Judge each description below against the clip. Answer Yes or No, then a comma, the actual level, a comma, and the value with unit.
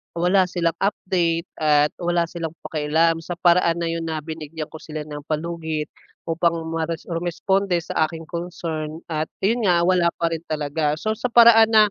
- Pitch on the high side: No, medium, 165 Hz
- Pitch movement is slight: Yes, narrow, 2.0 semitones